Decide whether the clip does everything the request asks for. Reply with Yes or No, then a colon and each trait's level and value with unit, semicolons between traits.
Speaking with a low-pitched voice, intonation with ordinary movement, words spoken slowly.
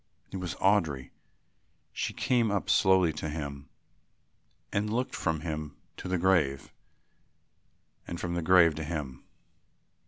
Yes: very low, 85 Hz; average, 3.9 semitones; slow, 130 wpm